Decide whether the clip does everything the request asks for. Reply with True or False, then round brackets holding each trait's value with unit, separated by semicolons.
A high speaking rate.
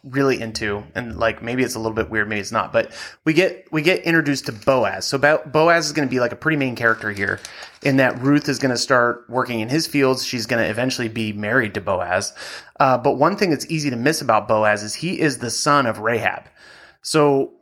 True (240 wpm)